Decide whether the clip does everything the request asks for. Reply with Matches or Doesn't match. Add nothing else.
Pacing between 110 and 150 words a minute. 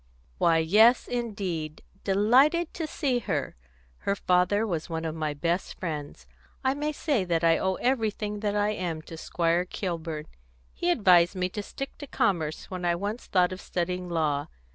Doesn't match